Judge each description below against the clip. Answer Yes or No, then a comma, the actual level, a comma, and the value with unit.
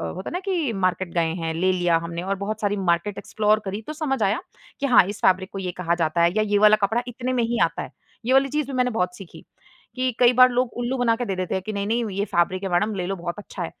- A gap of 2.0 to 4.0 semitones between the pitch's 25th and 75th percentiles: No, average, 4.9 semitones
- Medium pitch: No, high, 205 Hz